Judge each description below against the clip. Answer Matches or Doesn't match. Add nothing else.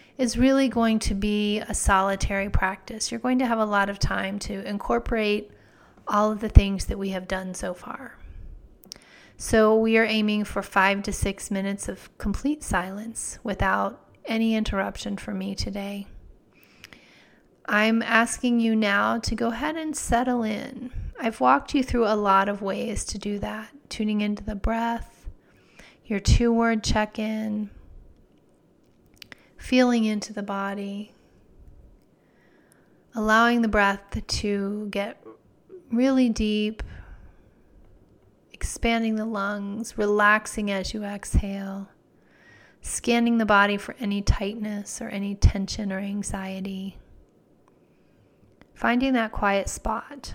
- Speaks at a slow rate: Matches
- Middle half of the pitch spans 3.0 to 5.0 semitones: Doesn't match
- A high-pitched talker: Matches